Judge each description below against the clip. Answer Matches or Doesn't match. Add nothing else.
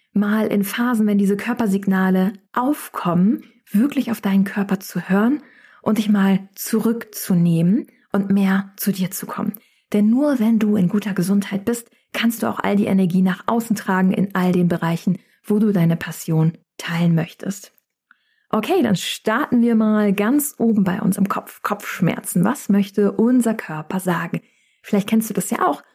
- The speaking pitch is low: Doesn't match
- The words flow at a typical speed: Matches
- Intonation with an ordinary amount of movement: Matches